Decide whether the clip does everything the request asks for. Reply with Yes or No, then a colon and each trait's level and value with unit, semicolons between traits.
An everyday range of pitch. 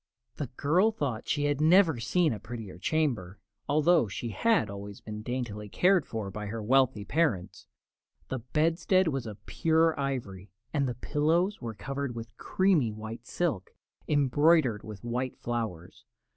No: wide, 6.5 semitones